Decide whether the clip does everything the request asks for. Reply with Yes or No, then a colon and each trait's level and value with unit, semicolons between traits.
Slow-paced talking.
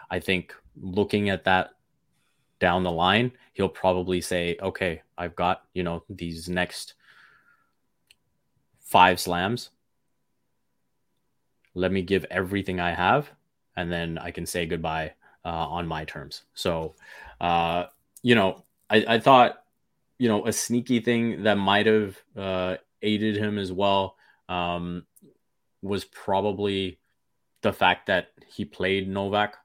Yes: slow, 130 wpm